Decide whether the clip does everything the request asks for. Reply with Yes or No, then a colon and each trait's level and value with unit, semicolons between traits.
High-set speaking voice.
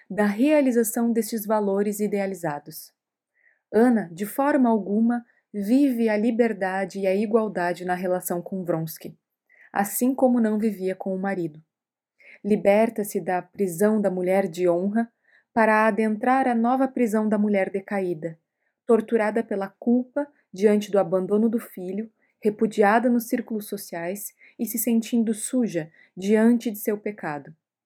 Yes: high, 210 Hz